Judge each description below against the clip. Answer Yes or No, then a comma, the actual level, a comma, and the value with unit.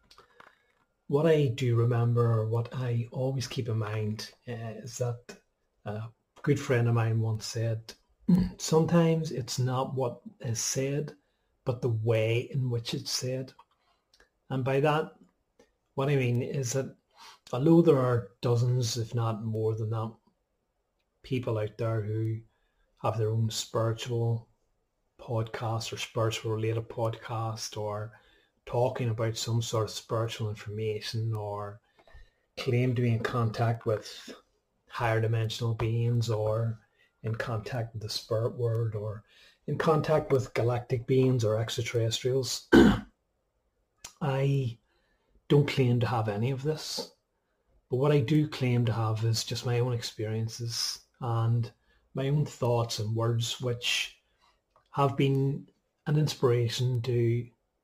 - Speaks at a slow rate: Yes, slow, 130 wpm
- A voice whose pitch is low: Yes, low, 120 Hz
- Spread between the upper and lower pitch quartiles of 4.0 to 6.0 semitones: No, average, 2.7 semitones